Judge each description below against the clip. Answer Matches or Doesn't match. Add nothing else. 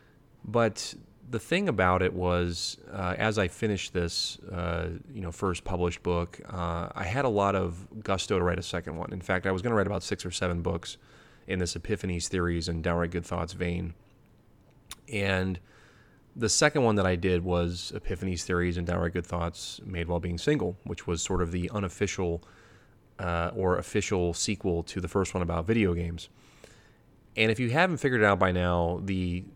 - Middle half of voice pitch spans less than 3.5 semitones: Matches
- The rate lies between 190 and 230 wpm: Matches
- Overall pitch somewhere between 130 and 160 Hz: Doesn't match